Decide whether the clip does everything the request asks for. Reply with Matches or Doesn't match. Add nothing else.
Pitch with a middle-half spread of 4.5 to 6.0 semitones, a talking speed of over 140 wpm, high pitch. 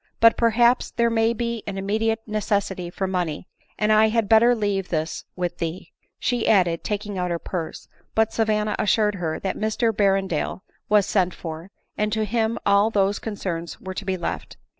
Doesn't match